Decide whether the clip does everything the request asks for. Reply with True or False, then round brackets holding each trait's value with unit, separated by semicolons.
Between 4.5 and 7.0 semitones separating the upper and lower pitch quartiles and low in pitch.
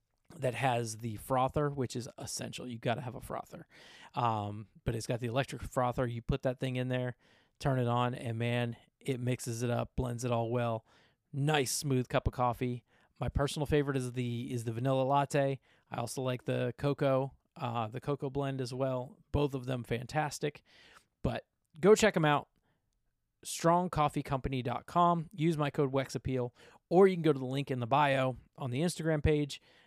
False (2.8 semitones; 130 Hz)